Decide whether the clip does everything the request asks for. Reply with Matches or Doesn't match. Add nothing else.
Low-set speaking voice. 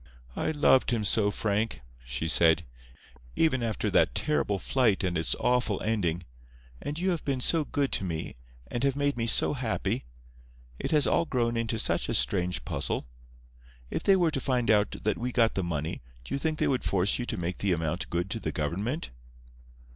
Matches